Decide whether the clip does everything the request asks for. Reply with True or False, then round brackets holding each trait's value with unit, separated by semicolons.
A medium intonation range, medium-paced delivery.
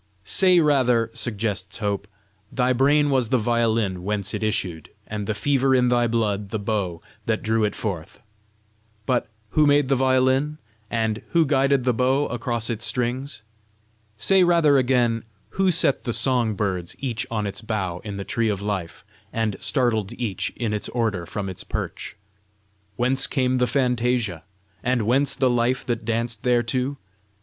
True (3.6 semitones; 160 wpm)